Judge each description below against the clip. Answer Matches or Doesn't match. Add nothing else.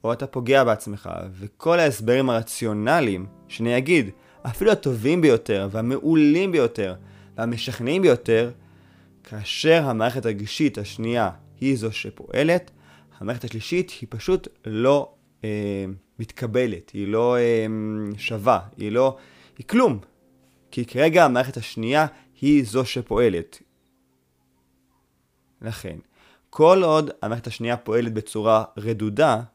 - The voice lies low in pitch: Matches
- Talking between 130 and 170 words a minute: Doesn't match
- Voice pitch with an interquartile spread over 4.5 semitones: Doesn't match